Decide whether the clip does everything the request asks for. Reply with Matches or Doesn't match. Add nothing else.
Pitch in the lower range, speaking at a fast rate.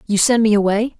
Doesn't match